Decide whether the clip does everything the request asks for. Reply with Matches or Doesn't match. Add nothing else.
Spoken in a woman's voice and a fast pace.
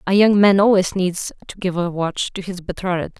Matches